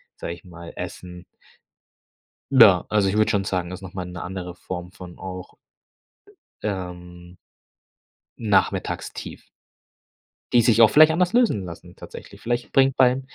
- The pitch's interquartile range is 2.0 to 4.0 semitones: No, average, 4.5 semitones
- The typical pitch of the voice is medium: No, very low, 95 Hz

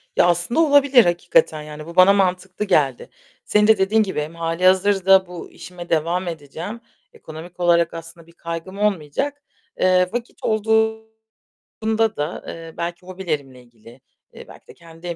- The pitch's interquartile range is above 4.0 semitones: No, average, 3.5 semitones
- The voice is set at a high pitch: No, medium, 175 Hz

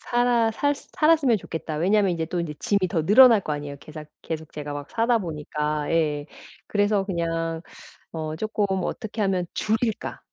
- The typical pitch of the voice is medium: Yes, medium, 180 Hz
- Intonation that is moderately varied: No, wide, 5.8 semitones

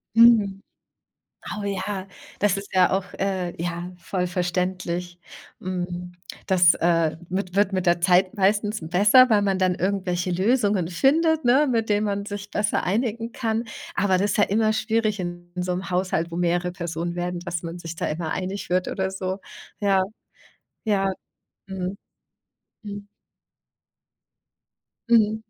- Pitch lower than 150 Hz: No, high, 190 Hz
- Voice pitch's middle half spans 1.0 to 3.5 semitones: Yes, average, 2.8 semitones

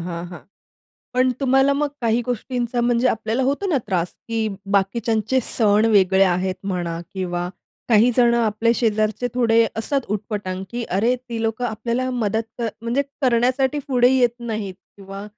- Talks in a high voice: Yes, high, 225 Hz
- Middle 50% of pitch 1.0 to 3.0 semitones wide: No, average, 3.4 semitones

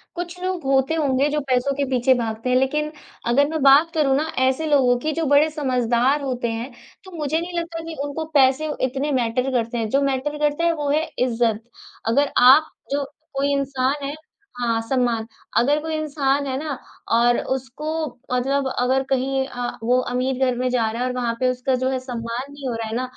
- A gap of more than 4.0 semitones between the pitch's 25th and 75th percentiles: No, average, 2.9 semitones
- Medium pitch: No, very high, 265 Hz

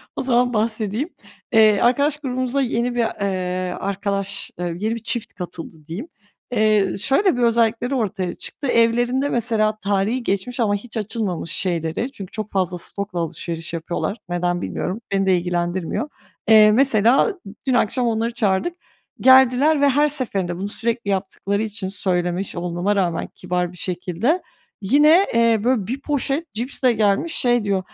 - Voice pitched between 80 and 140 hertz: No, high, 215 Hz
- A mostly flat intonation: No, average, 4.8 semitones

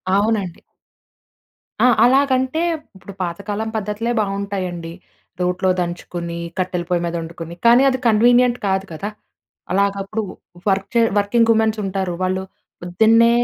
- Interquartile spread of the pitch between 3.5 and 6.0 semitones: Yes, average, 4.0 semitones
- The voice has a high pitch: Yes, high, 200 Hz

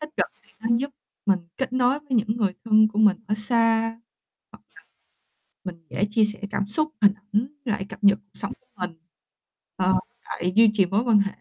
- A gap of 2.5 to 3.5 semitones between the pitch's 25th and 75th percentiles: Yes, average, 2.8 semitones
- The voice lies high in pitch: Yes, high, 215 Hz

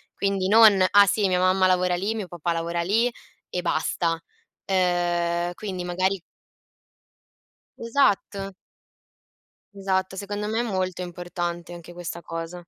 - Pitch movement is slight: Yes, narrow, 2.3 semitones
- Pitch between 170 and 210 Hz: Yes, medium, 185 Hz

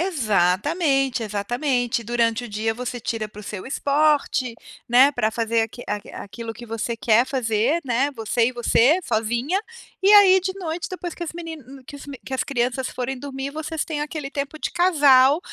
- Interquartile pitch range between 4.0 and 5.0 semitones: Yes, average, 4.7 semitones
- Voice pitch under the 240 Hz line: No, very high, 260 Hz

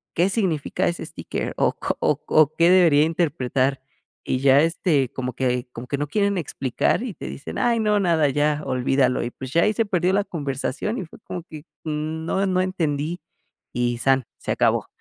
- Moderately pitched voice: Yes, medium, 155 Hz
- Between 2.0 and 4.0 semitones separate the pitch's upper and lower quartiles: No, average, 5.2 semitones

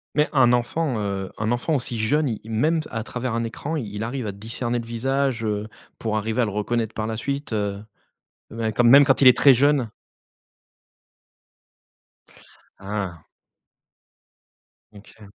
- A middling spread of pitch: Yes, average, 3.6 semitones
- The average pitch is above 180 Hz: No, low, 115 Hz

